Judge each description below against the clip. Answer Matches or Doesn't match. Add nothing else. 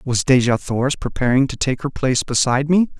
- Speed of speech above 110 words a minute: Matches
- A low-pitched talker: Matches